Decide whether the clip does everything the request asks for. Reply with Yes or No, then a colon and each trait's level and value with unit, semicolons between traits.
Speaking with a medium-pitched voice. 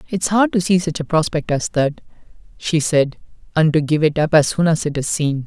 Yes: medium, 160 Hz